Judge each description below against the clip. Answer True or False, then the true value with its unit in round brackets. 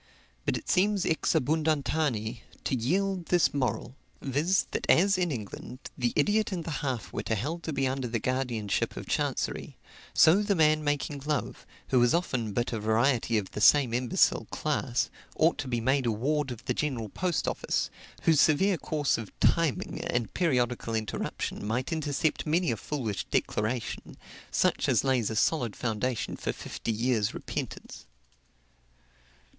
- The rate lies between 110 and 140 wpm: False (160 wpm)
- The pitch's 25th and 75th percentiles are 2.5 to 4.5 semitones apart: False (5.2 semitones)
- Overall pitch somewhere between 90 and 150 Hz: True (135 Hz)